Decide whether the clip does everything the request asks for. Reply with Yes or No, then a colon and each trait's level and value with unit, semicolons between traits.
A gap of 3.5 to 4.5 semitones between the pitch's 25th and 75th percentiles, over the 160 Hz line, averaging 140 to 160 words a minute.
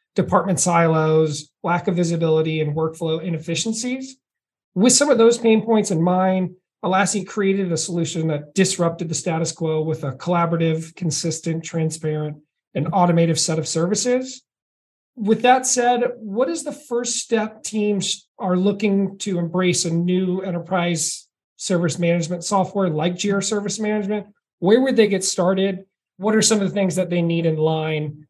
Yes: average, 4.1 semitones; medium, 185 Hz; average, 155 wpm